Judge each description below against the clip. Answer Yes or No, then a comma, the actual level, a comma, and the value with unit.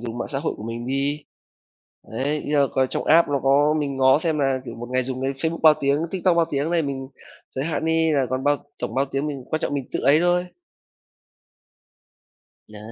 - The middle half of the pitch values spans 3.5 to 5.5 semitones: No, average, 2.8 semitones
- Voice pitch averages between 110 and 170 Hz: Yes, medium, 140 Hz